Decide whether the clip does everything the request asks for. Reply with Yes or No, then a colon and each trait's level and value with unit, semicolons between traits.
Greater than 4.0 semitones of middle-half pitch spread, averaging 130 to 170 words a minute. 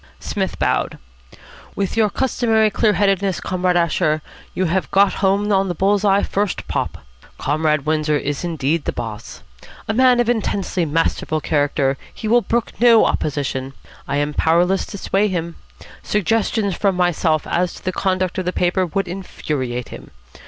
Yes: average, 4.5 semitones; average, 160 wpm